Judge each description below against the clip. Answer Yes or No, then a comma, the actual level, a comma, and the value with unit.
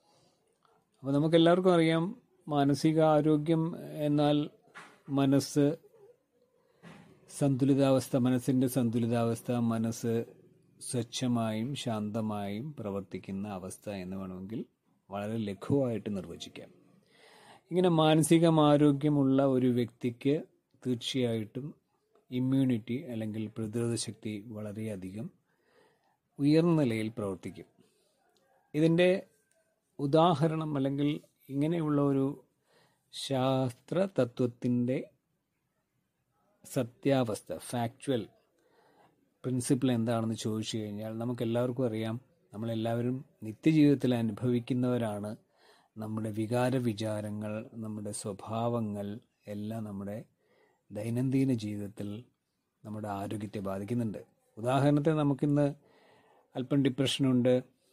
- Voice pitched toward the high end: No, low, 125 Hz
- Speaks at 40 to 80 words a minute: Yes, average, 70 wpm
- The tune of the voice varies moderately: Yes, average, 4.8 semitones